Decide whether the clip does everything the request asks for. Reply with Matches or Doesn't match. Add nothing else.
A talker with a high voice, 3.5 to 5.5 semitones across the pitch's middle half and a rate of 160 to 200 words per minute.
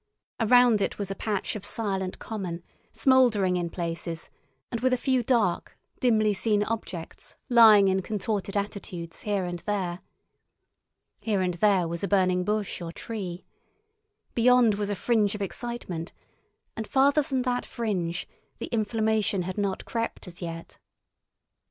Doesn't match